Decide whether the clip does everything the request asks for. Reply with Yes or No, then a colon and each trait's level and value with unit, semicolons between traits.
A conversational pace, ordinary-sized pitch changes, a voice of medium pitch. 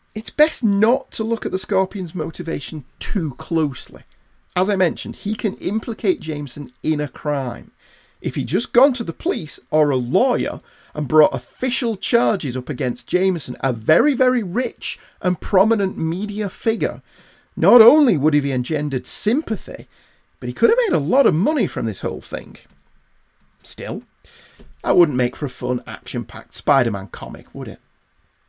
No: average, 170 wpm; wide, 7.7 semitones; medium, 165 Hz